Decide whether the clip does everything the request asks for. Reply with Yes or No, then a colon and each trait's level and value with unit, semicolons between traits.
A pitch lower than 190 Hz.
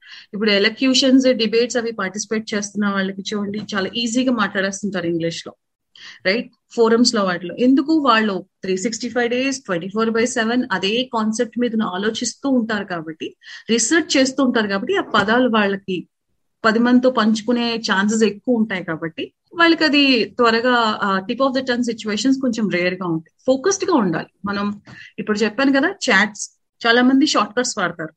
No: high, 225 Hz